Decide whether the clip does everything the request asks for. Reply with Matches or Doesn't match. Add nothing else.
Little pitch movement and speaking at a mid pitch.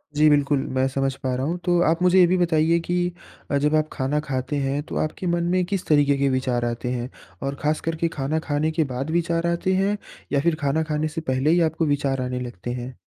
Doesn't match